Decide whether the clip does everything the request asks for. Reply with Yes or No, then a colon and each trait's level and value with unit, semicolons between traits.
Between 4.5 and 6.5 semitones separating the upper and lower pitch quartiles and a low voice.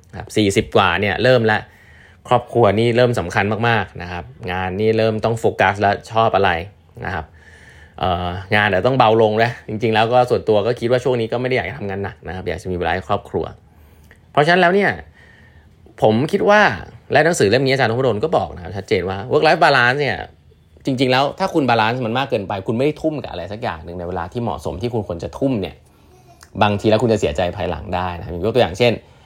Yes: average, 4.9 semitones; low, 110 Hz